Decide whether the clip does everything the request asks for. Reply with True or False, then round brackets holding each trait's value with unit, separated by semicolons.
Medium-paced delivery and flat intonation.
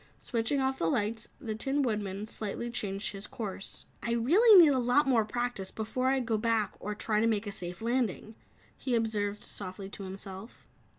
False (185 wpm; 3.3 semitones)